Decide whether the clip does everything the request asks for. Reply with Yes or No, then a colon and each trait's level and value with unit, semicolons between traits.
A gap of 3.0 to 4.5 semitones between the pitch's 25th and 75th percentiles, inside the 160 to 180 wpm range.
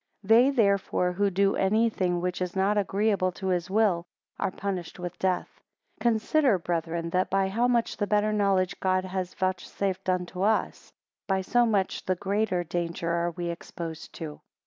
No: narrow, 2.5 semitones; average, 175 wpm